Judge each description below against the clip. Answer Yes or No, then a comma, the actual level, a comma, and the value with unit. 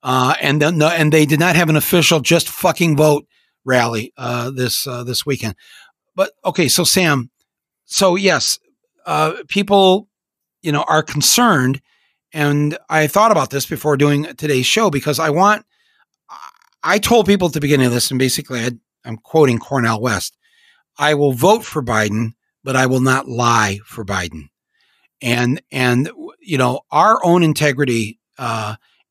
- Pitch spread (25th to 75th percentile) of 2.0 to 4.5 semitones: No, wide, 5.6 semitones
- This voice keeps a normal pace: Yes, average, 160 wpm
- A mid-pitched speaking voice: Yes, medium, 150 Hz